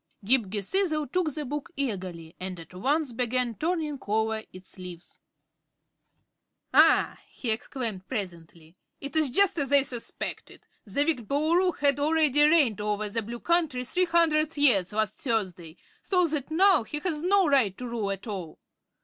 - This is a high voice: Yes, very high, 255 Hz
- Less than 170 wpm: Yes, average, 160 wpm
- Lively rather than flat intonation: Yes, wide, 7.0 semitones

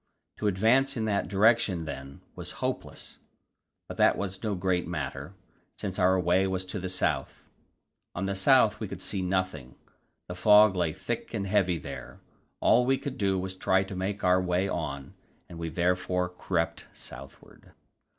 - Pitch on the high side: No, very low, 95 Hz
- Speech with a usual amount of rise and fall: No, narrow, 2.1 semitones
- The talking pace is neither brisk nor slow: Yes, average, 170 wpm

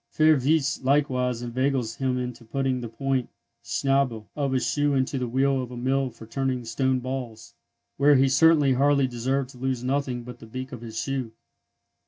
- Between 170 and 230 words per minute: Yes, average, 180 wpm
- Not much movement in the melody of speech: Yes, narrow, 1.8 semitones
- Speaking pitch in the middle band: No, low, 130 Hz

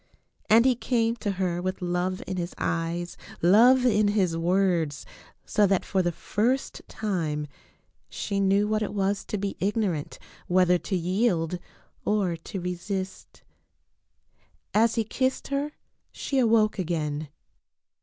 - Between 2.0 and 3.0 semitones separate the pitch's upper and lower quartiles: No, average, 3.6 semitones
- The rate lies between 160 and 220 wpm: No, average, 140 wpm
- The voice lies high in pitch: Yes, high, 195 Hz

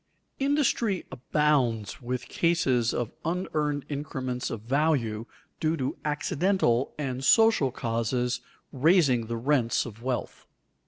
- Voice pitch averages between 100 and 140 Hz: Yes, low, 135 Hz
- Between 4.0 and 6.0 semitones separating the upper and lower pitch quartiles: Yes, average, 4.5 semitones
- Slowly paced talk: Yes, slow, 110 wpm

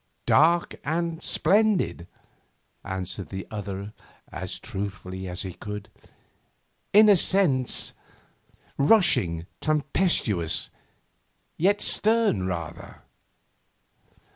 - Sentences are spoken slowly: Yes, slow, 85 wpm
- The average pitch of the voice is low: Yes, low, 110 Hz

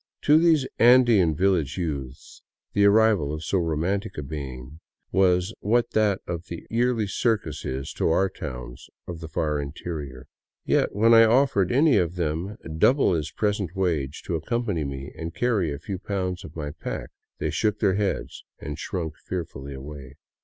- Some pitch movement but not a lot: No, wide, 5.7 semitones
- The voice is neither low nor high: No, very low, 90 Hz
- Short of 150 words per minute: No, average, 165 wpm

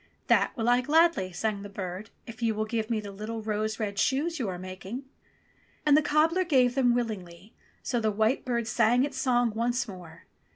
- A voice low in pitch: No, high, 225 Hz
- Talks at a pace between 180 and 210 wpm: Yes, average, 200 wpm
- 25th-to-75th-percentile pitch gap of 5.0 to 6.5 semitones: No, average, 3.6 semitones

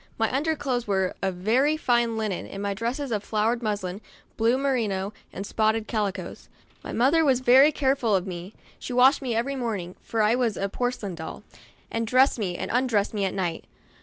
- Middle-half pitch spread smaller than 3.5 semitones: No, average, 4.2 semitones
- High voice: Yes, high, 225 Hz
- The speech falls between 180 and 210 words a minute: Yes, average, 195 wpm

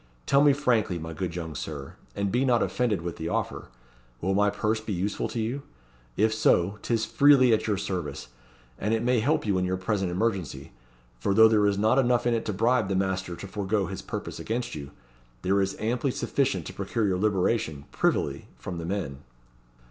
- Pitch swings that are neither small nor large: Yes, average, 3.9 semitones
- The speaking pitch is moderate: No, low, 105 Hz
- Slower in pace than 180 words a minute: No, average, 200 wpm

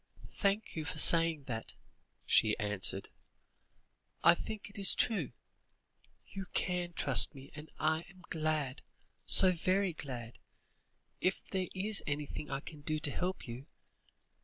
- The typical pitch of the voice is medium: Yes, medium, 160 Hz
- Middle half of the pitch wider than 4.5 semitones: Yes, average, 4.9 semitones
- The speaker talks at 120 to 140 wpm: Yes, slow, 135 wpm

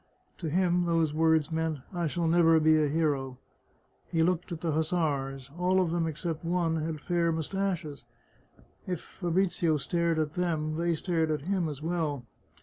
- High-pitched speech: No, medium, 165 Hz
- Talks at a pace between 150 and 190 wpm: Yes, average, 175 wpm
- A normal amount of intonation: No, narrow, 2.1 semitones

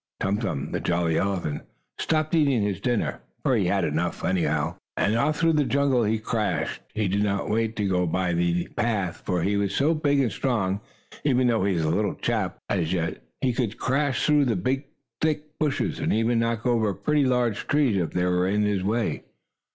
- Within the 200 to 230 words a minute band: Yes, fast, 205 wpm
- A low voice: Yes, low, 110 Hz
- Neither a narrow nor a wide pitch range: No, wide, 5.8 semitones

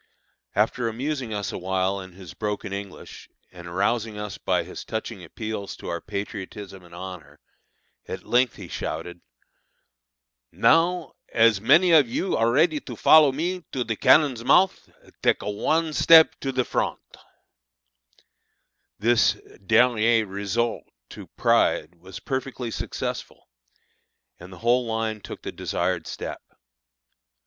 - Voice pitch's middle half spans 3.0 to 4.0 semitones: No, average, 5.0 semitones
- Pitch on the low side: Yes, low, 110 Hz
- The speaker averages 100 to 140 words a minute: Yes, slow, 135 wpm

